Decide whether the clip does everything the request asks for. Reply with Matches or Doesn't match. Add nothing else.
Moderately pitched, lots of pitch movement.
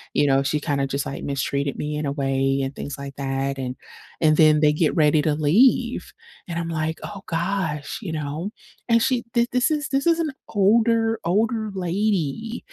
Matches